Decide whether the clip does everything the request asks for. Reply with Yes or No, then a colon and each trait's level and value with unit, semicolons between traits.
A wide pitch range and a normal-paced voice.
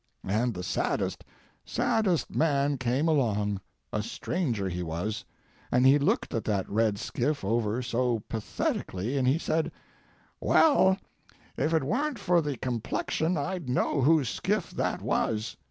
No: wide, 6.5 semitones; slow, 130 wpm